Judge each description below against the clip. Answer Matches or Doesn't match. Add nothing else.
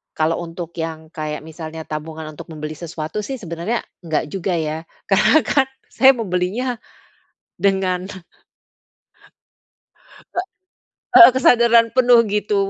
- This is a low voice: Doesn't match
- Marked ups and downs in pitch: Matches